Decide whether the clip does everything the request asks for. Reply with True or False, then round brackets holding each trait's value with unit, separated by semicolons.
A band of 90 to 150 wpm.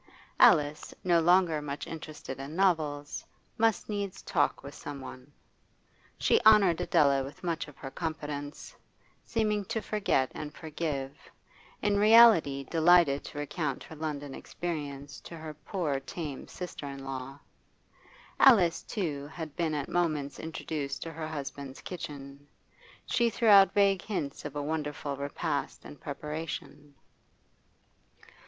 True (135 wpm)